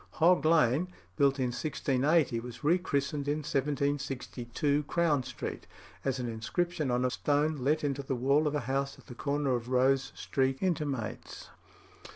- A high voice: No, medium, 140 Hz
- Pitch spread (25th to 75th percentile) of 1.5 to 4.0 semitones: Yes, average, 2.8 semitones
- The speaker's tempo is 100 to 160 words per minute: Yes, average, 155 wpm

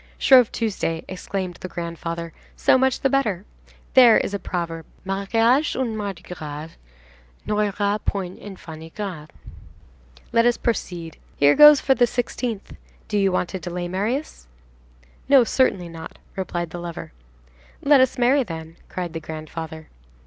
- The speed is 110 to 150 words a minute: Yes, average, 140 wpm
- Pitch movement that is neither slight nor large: No, wide, 5.7 semitones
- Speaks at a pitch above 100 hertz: Yes, high, 190 Hz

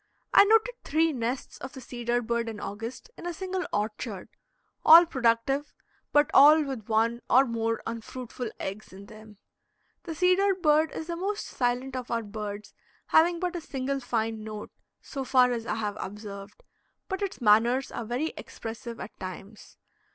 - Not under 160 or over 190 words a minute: Yes, average, 165 wpm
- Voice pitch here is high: Yes, high, 245 Hz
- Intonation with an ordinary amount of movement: No, wide, 5.9 semitones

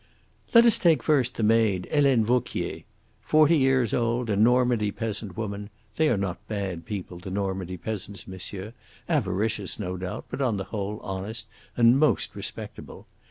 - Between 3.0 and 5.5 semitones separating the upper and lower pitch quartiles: Yes, average, 4.2 semitones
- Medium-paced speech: Yes, average, 160 wpm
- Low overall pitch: Yes, low, 110 Hz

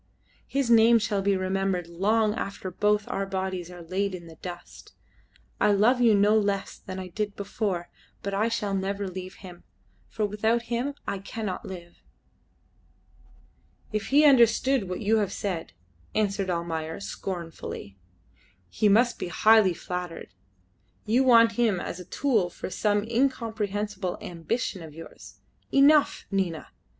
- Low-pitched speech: No, high, 200 Hz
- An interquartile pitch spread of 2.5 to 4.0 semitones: Yes, average, 3.5 semitones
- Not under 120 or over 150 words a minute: Yes, average, 145 wpm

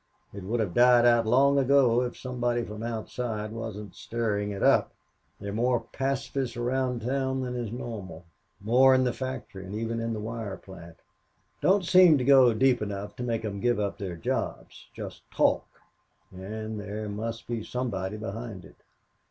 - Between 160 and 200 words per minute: Yes, average, 175 wpm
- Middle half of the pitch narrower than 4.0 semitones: Yes, average, 3.1 semitones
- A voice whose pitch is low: Yes, low, 115 Hz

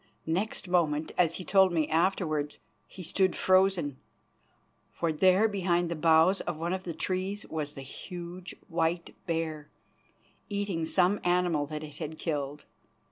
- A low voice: No, medium, 170 Hz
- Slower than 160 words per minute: Yes, average, 145 wpm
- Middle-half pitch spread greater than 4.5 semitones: No, average, 3.0 semitones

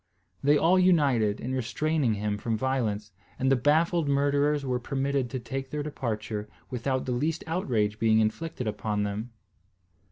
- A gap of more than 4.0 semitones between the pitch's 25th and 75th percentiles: Yes, average, 5.0 semitones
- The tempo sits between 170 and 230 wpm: No, average, 155 wpm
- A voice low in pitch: Yes, low, 130 Hz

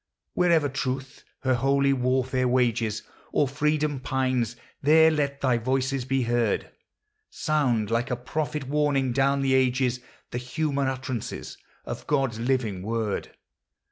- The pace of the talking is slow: Yes, slow, 130 wpm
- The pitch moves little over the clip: Yes, narrow, 2.3 semitones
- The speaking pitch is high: No, low, 130 Hz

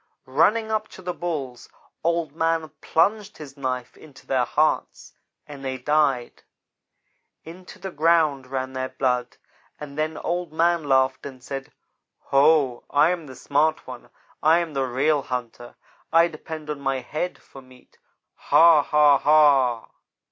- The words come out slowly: No, average, 150 wpm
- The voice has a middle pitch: Yes, medium, 150 Hz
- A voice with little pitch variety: No, average, 3.7 semitones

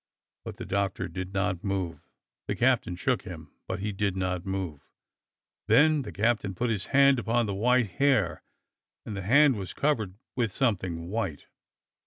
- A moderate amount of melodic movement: Yes, average, 4.5 semitones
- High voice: No, low, 100 Hz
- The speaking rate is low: No, average, 170 wpm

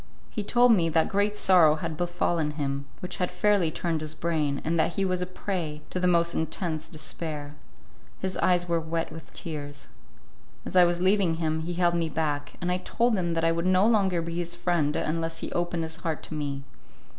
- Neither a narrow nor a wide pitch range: No, narrow, 2.3 semitones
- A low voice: No, medium, 170 Hz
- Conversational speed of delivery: No, fast, 210 wpm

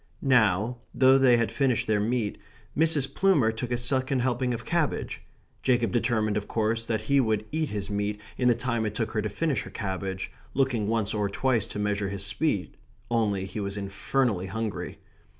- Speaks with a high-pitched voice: No, low, 115 Hz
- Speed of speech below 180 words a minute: No, average, 185 wpm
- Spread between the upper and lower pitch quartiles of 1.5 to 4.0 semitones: Yes, average, 3.7 semitones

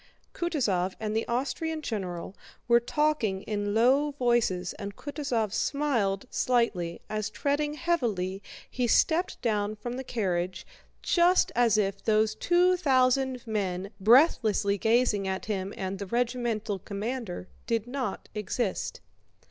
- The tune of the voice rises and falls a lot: No, average, 4.6 semitones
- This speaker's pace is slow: Yes, slow, 125 wpm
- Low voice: No, high, 225 Hz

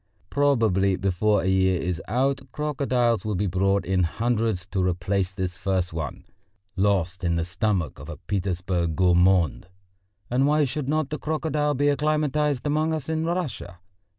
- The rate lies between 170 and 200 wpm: No, average, 155 wpm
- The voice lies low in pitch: Yes, low, 105 Hz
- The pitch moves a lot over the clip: Yes, wide, 7.7 semitones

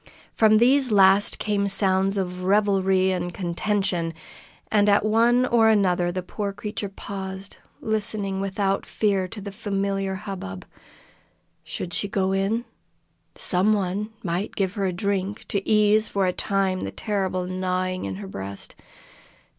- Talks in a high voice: Yes, high, 195 Hz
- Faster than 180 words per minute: No, average, 145 wpm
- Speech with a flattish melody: Yes, narrow, 2.0 semitones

